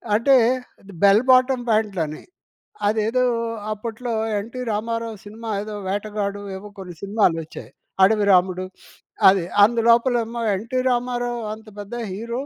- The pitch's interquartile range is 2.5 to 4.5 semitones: Yes, average, 2.9 semitones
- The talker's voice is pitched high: Yes, high, 215 Hz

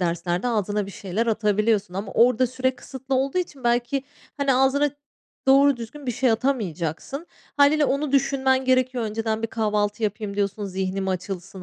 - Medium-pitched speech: No, high, 230 Hz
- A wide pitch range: No, average, 4.7 semitones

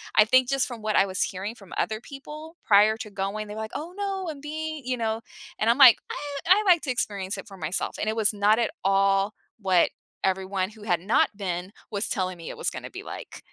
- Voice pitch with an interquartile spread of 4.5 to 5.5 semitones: Yes, average, 4.9 semitones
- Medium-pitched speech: No, high, 215 Hz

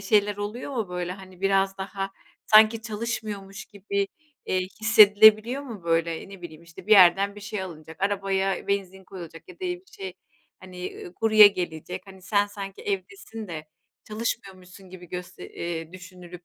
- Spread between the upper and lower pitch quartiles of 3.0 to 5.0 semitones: No, narrow, 2.6 semitones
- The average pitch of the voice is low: No, high, 195 Hz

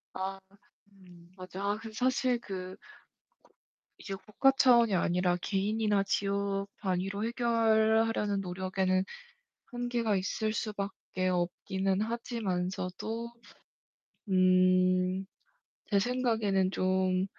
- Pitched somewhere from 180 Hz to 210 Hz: Yes, high, 195 Hz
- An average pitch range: Yes, average, 3.1 semitones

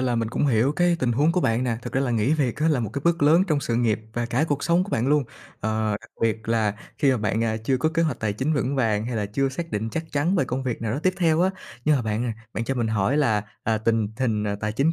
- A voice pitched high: No, low, 125 Hz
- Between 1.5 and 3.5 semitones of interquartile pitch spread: No, average, 5.0 semitones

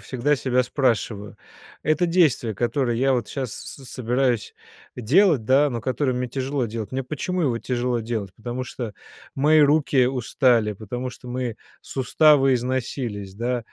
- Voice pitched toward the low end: Yes, low, 125 Hz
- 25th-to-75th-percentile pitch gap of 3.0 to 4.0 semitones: No, narrow, 2.6 semitones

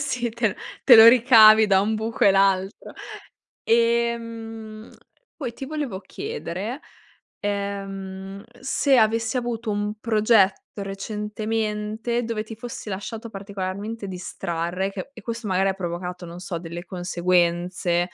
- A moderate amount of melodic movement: Yes, average, 3.2 semitones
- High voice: Yes, high, 210 Hz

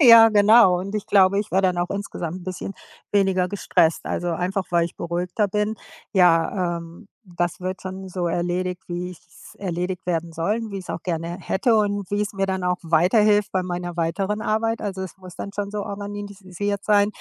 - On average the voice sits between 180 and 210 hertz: Yes, high, 190 Hz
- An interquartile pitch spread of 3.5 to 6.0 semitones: No, narrow, 2.5 semitones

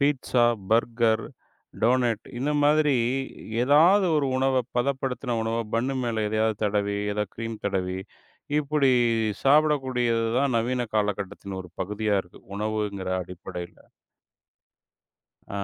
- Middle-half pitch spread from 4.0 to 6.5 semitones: Yes, average, 4.3 semitones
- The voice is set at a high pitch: No, low, 115 Hz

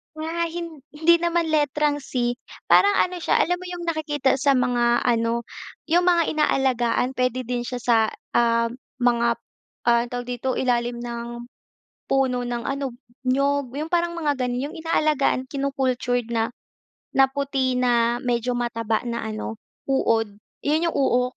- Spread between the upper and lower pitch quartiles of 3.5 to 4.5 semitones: Yes, average, 3.8 semitones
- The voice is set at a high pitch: Yes, very high, 255 Hz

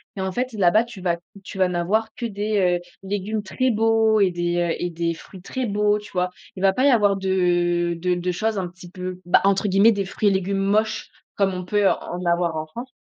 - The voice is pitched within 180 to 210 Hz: Yes, high, 190 Hz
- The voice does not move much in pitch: No, average, 3.0 semitones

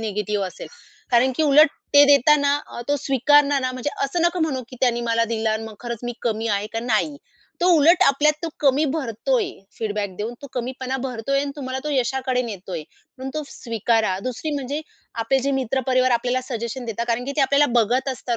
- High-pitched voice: Yes, very high, 255 Hz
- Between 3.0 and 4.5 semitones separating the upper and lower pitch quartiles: Yes, average, 3.5 semitones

